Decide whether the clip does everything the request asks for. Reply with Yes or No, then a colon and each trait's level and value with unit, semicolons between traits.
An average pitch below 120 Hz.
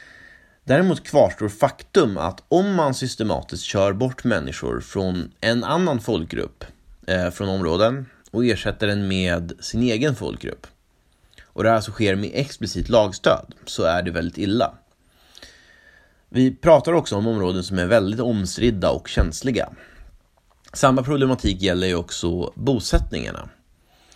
Yes: low, 110 Hz